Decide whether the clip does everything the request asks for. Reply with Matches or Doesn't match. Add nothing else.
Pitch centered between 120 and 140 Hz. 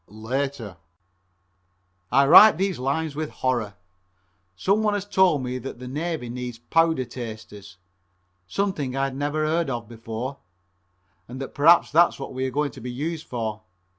Matches